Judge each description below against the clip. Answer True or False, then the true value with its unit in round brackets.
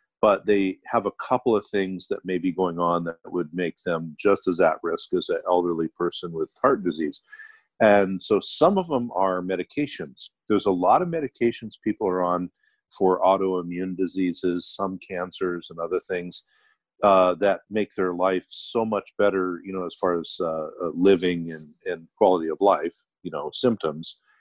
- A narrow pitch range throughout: True (2.0 semitones)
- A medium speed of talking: True (180 wpm)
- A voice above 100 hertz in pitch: False (95 Hz)